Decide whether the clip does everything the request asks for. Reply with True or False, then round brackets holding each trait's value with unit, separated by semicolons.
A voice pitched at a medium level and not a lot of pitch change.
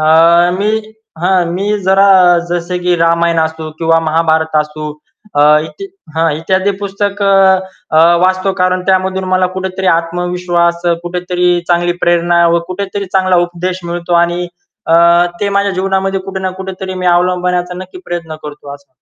True (180 Hz; 1.9 semitones)